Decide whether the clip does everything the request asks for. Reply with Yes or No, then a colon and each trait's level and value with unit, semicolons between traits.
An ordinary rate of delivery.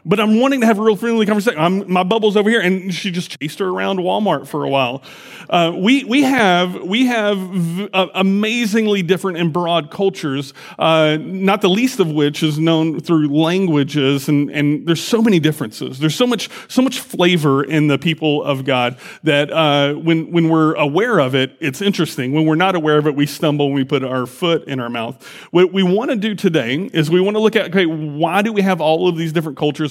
No: fast, 225 wpm